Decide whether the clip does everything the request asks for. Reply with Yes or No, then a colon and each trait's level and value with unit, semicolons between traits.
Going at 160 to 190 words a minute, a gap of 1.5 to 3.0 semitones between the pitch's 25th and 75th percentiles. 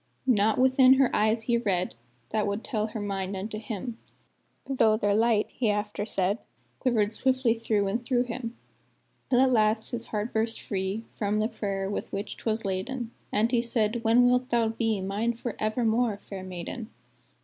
Yes: average, 175 wpm; narrow, 2.5 semitones